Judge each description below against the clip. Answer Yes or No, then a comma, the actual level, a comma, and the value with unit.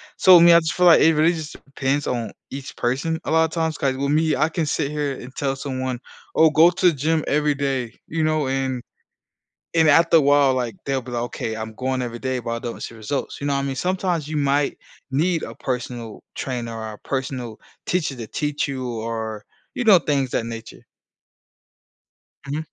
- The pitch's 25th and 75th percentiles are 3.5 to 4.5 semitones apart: Yes, average, 4.0 semitones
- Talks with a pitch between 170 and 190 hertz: No, medium, 140 Hz